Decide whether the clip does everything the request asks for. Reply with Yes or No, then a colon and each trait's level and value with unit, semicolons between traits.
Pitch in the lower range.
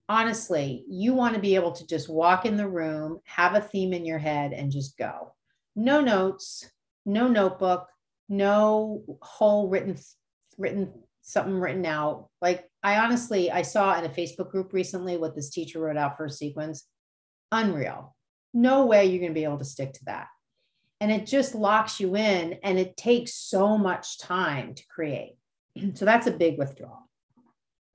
No: medium, 185 Hz